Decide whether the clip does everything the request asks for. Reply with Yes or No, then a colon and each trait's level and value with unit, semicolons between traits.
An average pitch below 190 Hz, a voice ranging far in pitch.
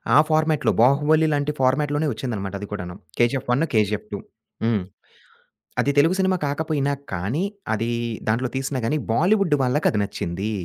Yes: low, 135 Hz; wide, 6.0 semitones